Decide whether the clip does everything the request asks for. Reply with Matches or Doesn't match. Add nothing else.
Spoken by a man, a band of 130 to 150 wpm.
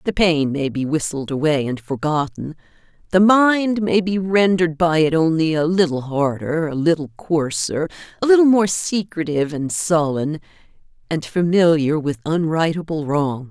Doesn't match